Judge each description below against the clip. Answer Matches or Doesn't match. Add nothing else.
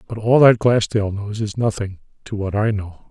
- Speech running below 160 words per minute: Doesn't match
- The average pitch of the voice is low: Matches